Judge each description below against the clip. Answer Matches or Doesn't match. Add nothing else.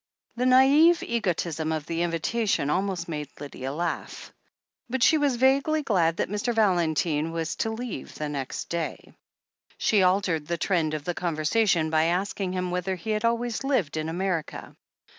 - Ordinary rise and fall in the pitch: Doesn't match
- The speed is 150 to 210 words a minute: Matches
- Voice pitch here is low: Doesn't match